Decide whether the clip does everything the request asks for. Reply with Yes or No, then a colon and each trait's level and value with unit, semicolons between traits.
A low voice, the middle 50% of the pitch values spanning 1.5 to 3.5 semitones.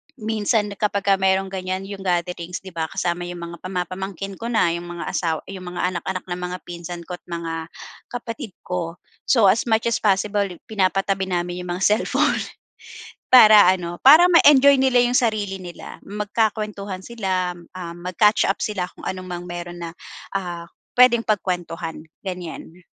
No: high, 190 Hz; average, 3.1 semitones